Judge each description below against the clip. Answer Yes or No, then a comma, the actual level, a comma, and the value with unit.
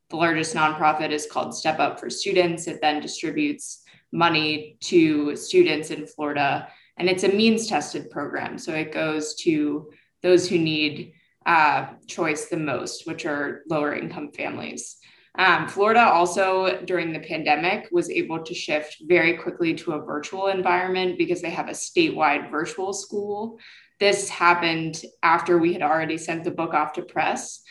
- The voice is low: No, medium, 170 Hz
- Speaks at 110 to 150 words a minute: No, average, 160 wpm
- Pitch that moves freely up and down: No, average, 3.9 semitones